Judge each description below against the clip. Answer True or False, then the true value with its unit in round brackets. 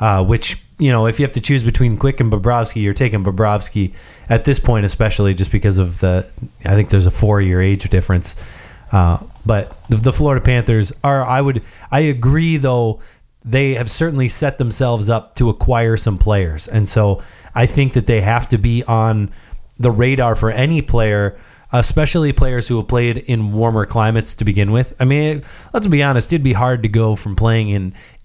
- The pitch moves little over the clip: False (3.8 semitones)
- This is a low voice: True (115 Hz)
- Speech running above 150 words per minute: True (195 wpm)